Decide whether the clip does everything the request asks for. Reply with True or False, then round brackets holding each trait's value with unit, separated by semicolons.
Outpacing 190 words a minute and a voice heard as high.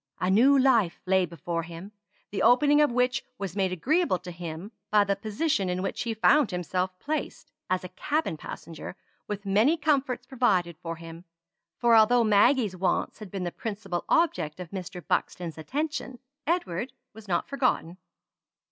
False (165 wpm; 200 Hz)